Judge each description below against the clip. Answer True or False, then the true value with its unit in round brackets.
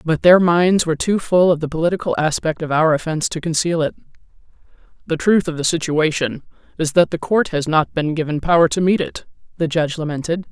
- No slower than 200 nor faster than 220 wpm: True (205 wpm)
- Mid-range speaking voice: True (165 Hz)